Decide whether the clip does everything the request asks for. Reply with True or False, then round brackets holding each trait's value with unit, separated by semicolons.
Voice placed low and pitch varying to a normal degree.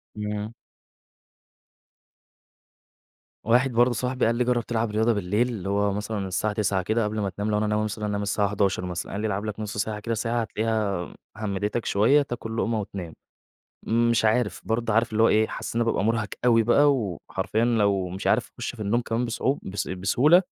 False (110 Hz; 2.3 semitones)